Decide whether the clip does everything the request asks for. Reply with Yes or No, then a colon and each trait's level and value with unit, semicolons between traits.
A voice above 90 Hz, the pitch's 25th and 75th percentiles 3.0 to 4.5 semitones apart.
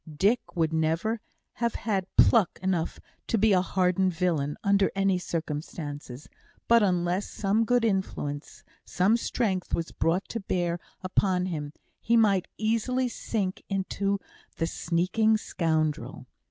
Yes: medium, 185 Hz; average, 4.2 semitones